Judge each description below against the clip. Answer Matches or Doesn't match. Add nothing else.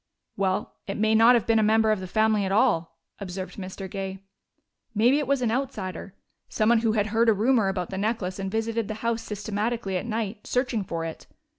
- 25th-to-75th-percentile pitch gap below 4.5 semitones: Matches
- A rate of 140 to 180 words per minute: Doesn't match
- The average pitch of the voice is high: Matches